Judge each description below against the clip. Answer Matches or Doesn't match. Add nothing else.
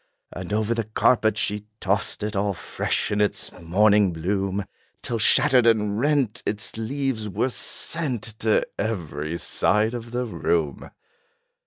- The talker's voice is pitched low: Matches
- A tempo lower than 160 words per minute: Matches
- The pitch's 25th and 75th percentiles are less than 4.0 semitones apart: Matches